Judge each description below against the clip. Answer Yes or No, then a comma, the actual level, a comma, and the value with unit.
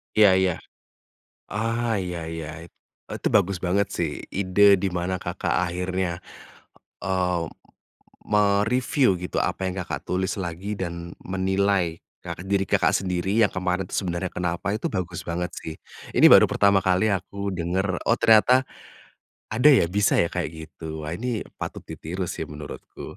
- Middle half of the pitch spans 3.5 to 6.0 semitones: No, narrow, 2.4 semitones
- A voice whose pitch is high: No, very low, 95 Hz